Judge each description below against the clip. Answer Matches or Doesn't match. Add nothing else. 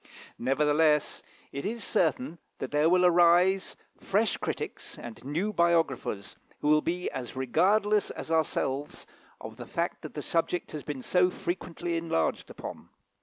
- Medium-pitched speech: Matches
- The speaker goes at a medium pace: Matches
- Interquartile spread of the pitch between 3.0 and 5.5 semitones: Matches